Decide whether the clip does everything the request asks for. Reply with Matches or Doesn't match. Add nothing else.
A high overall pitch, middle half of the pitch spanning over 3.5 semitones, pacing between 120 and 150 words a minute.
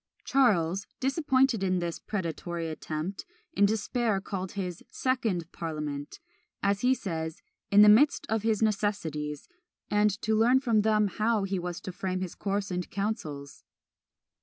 Matches